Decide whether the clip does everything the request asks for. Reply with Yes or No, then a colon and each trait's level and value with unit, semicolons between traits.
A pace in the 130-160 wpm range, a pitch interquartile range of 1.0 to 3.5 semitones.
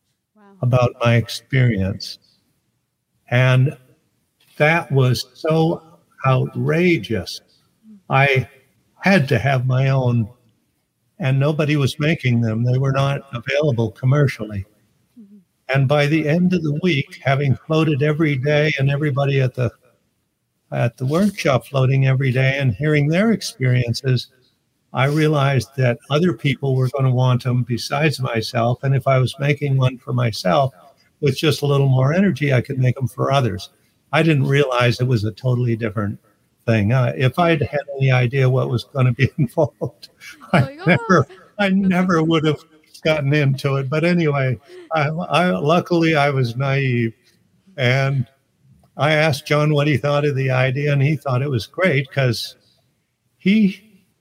Yes: average, 155 wpm; average, 3.2 semitones